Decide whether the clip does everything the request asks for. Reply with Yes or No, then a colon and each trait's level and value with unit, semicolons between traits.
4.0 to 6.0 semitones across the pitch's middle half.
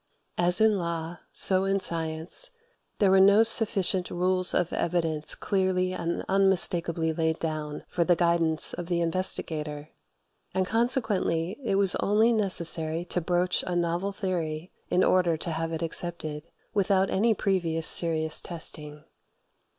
No: average, 2.8 semitones